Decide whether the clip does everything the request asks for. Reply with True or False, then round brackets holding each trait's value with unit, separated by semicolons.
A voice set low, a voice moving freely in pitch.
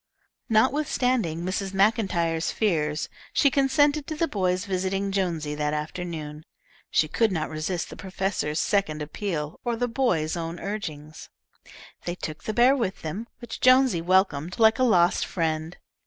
False (185 Hz; 6.0 semitones)